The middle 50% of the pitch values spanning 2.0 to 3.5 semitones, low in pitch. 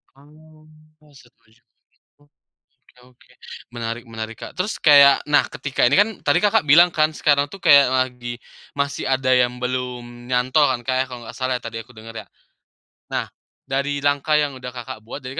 Yes: average, 2.9 semitones; low, 130 Hz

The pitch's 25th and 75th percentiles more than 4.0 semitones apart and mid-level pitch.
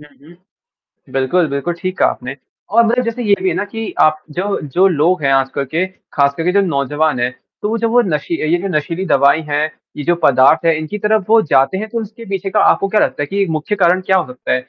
Yes: wide, 5.6 semitones; medium, 175 Hz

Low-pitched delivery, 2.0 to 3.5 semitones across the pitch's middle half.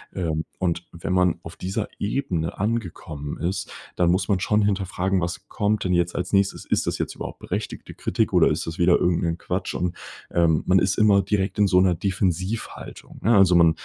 Yes: very low, 90 Hz; narrow, 2.6 semitones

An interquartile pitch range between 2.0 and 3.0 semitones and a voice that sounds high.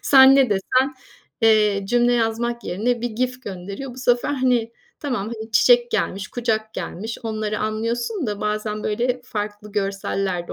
Yes: average, 2.7 semitones; high, 225 Hz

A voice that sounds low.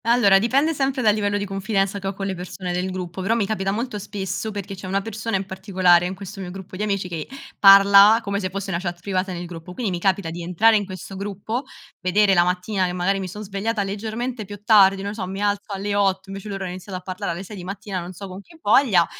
No: high, 195 Hz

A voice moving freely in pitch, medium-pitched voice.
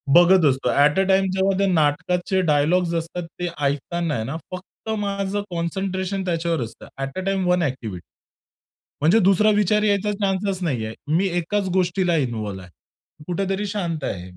No: average, 4.1 semitones; medium, 180 Hz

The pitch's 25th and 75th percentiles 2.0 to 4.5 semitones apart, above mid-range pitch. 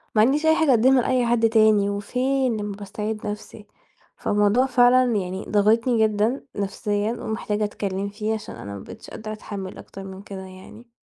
Yes: average, 2.8 semitones; high, 215 Hz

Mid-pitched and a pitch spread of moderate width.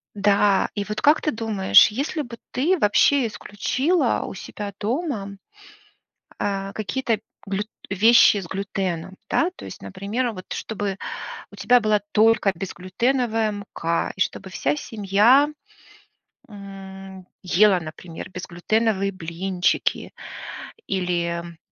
No: high, 200 Hz; average, 3.1 semitones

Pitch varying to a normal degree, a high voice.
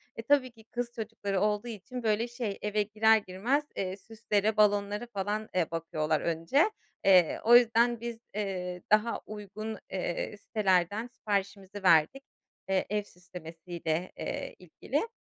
Yes: average, 3.4 semitones; high, 210 Hz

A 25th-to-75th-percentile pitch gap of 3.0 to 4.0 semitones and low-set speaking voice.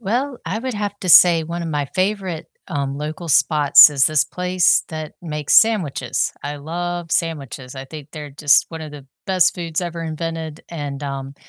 No: average, 3.5 semitones; medium, 160 Hz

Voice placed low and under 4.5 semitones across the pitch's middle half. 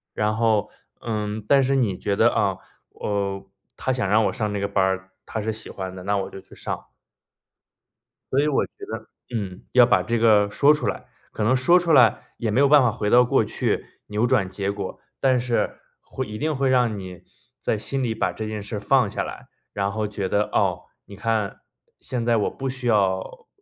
Yes: low, 110 Hz; average, 3.7 semitones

